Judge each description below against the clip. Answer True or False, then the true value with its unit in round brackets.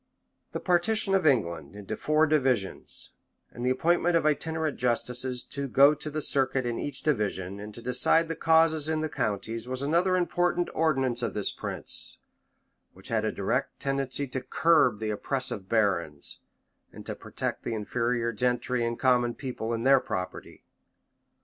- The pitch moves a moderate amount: True (4.9 semitones)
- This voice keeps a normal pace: True (160 wpm)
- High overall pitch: False (130 Hz)